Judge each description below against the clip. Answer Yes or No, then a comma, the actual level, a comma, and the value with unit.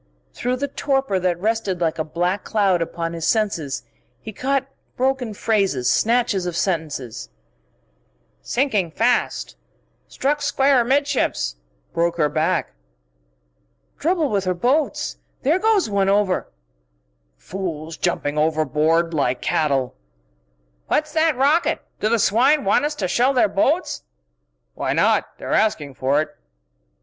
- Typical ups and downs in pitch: No, wide, 8.7 semitones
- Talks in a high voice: Yes, high, 195 Hz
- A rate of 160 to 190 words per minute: No, slow, 135 wpm